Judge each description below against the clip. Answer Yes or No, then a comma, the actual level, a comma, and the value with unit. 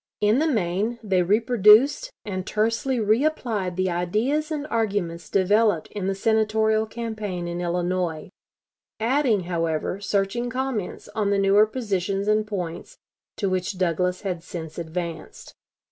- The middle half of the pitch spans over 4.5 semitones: No, average, 3.7 semitones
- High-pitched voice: Yes, high, 205 Hz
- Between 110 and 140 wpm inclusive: Yes, slow, 135 wpm